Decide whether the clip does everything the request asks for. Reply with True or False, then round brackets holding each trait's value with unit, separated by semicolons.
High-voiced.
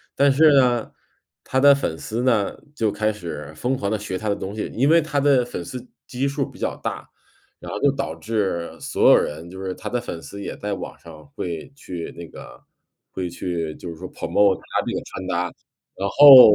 False (105 Hz)